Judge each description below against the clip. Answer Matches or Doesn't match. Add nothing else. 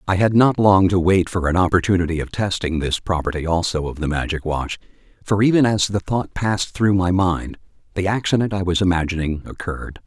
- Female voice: Doesn't match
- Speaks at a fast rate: Doesn't match